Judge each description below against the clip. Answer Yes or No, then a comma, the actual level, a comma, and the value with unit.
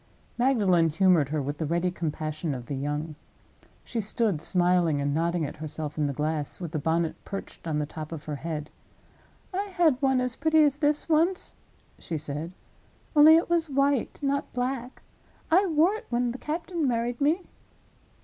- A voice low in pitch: No, medium, 180 Hz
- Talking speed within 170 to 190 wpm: Yes, average, 175 wpm